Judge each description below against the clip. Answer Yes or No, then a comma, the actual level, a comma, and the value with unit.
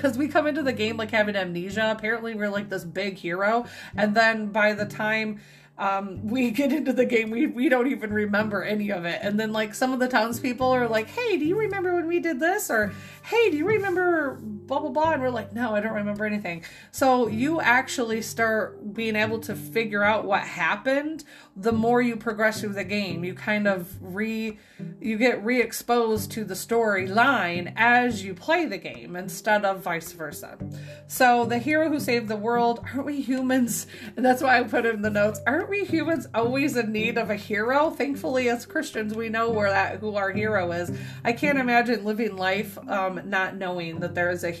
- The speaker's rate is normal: No, fast, 210 wpm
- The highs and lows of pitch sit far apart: No, average, 4.0 semitones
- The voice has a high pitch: Yes, high, 225 Hz